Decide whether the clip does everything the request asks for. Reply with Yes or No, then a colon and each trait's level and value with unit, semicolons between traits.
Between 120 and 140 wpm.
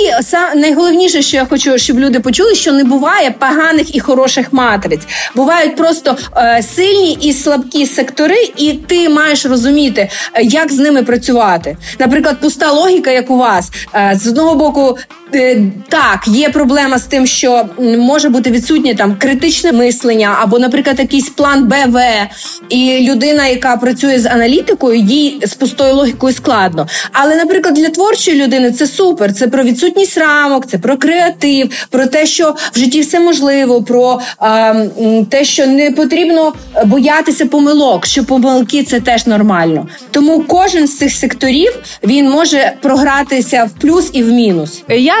No: average, 150 wpm